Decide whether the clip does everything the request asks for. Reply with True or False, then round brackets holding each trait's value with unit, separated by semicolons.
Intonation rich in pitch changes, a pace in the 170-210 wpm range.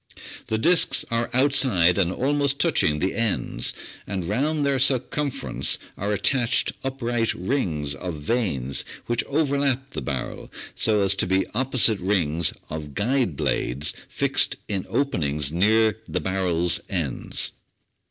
False (7.5 semitones; 135 wpm)